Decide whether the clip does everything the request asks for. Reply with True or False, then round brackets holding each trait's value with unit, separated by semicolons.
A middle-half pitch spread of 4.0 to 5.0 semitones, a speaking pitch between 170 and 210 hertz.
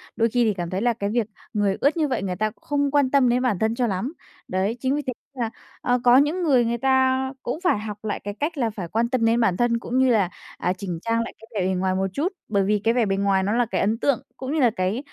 False (4.4 semitones; 230 Hz)